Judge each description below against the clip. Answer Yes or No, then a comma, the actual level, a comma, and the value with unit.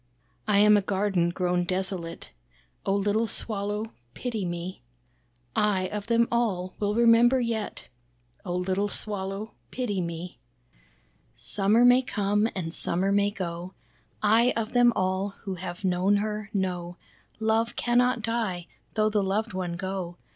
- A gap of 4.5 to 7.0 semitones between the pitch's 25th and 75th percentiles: No, average, 3.0 semitones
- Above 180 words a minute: No, average, 140 wpm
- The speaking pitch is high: Yes, high, 200 Hz